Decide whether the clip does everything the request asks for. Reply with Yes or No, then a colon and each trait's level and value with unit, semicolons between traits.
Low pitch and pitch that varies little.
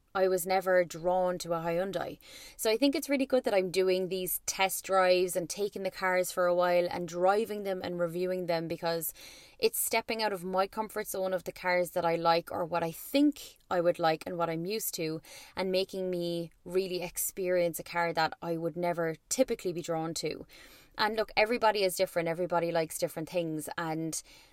No: medium, 180 Hz; narrow, 2.1 semitones